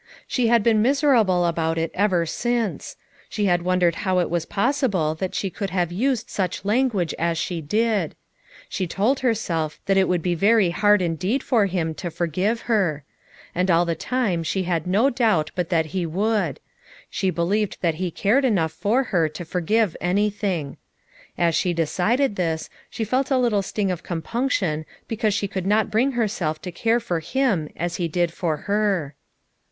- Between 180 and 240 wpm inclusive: Yes, average, 185 wpm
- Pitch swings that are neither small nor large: Yes, average, 4.5 semitones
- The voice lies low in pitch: No, medium, 185 Hz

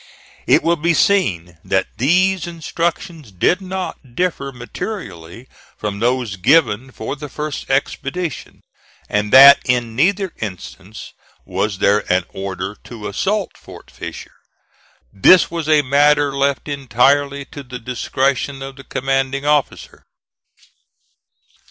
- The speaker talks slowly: Yes, slow, 120 wpm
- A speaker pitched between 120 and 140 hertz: Yes, low, 135 Hz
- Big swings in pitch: Yes, wide, 5.8 semitones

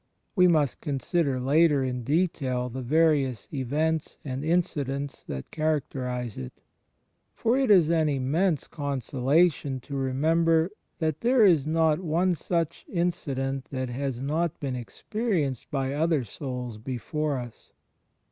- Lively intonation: No, average, 3.9 semitones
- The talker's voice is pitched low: No, medium, 145 Hz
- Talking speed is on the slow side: Yes, slow, 130 wpm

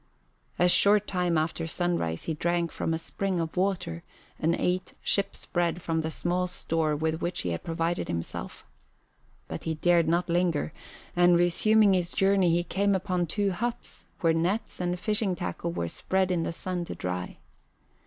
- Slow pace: No, average, 175 wpm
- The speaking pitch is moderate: Yes, medium, 175 Hz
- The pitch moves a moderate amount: No, narrow, 2.3 semitones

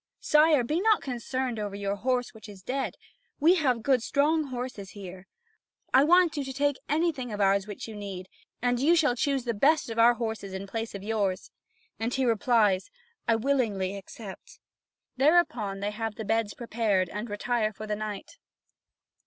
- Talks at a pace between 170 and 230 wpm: Yes, average, 180 wpm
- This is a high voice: Yes, high, 230 Hz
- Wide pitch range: No, average, 4.7 semitones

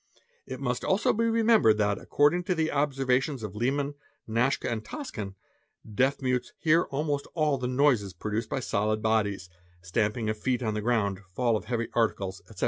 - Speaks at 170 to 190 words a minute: Yes, average, 175 wpm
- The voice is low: Yes, low, 125 Hz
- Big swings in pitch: No, average, 4.9 semitones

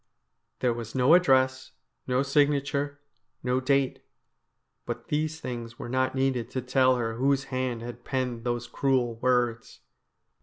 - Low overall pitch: Yes, low, 130 Hz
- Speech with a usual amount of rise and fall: No, narrow, 2.0 semitones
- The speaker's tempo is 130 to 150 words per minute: Yes, average, 140 wpm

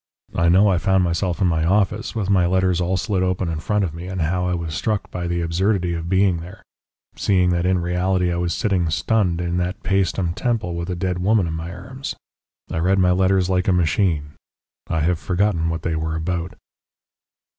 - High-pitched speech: No, very low, 90 Hz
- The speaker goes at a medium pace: No, fast, 210 wpm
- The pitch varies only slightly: Yes, narrow, 2.0 semitones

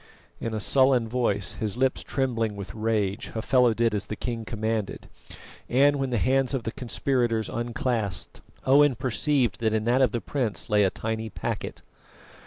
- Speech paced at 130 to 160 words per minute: No, average, 170 wpm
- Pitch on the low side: Yes, low, 115 Hz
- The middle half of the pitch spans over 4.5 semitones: No, average, 2.9 semitones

